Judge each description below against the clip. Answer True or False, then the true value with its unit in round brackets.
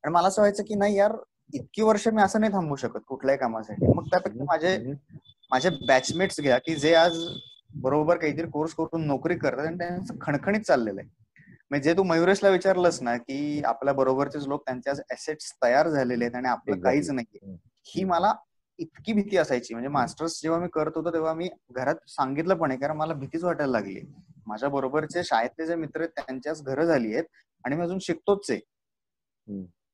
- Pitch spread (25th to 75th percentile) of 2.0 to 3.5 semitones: False (4.7 semitones)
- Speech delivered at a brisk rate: True (180 wpm)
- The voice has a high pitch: False (155 Hz)